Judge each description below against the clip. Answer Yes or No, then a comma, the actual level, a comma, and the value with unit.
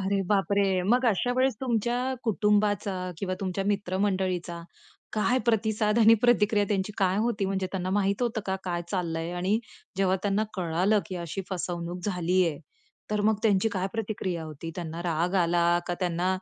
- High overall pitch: Yes, high, 195 Hz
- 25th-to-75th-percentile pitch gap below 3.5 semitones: Yes, average, 2.9 semitones